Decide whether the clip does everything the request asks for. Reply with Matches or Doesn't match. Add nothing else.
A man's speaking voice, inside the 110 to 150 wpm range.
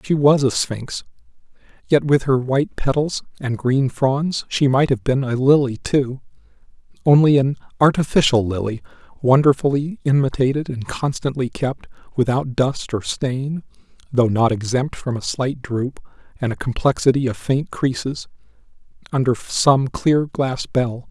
Matches